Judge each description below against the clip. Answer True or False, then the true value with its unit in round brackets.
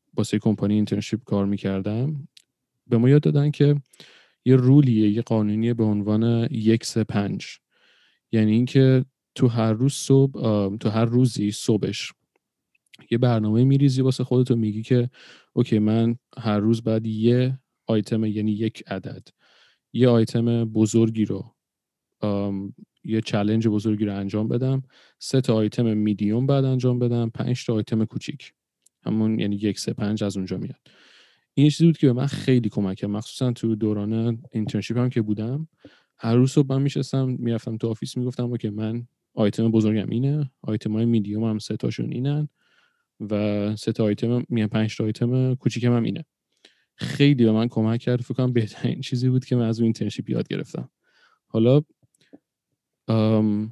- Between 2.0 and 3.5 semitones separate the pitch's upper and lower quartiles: True (2.9 semitones)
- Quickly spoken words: True (160 wpm)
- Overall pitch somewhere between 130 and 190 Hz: False (115 Hz)